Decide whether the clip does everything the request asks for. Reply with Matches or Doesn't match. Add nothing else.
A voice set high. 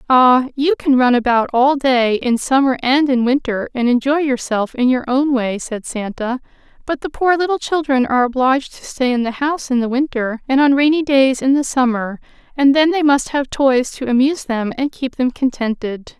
Matches